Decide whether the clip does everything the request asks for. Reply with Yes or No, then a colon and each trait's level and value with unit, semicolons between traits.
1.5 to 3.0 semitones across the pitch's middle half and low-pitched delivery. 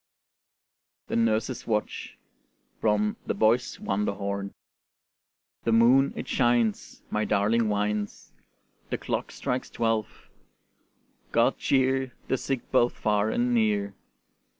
Yes: narrow, 2.6 semitones; low, 110 Hz